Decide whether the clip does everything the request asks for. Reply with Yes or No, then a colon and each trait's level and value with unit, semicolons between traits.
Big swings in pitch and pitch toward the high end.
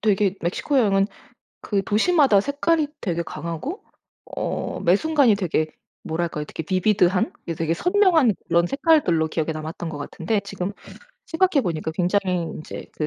Yes: wide, 8.4 semitones; high, 195 Hz